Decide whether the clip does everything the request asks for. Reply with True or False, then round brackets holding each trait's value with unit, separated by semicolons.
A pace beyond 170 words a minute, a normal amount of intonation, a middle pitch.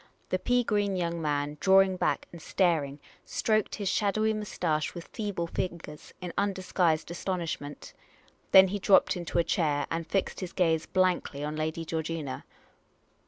False (150 wpm; 3.4 semitones; 175 Hz)